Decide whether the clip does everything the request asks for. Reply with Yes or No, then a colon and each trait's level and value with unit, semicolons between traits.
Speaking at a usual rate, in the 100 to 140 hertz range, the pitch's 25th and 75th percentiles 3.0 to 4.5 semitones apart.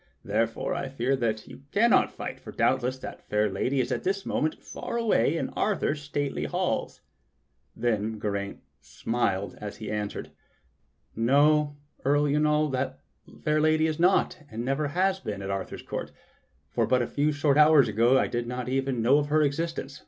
No: average, 170 wpm; low, 135 Hz; average, 5.1 semitones